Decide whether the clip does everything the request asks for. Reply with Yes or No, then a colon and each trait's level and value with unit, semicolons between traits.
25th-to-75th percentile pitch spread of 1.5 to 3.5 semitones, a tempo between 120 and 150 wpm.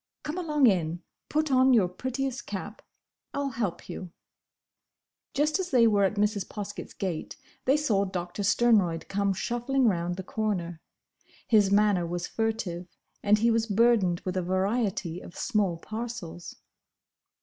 No: average, 4.7 semitones; average, 145 wpm